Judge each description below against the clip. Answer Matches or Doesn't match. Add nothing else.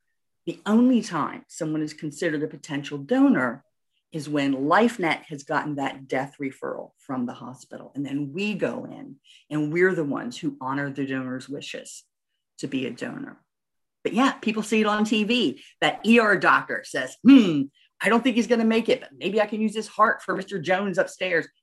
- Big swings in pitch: Matches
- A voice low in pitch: Doesn't match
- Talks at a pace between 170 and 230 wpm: Matches